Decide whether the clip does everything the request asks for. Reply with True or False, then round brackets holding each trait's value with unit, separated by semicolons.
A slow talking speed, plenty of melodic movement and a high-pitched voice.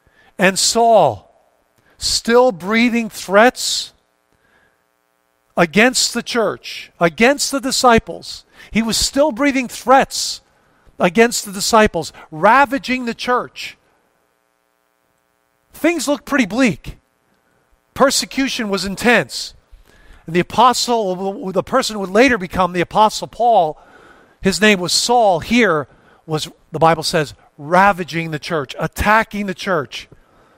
True (110 wpm; 7.8 semitones; 195 Hz)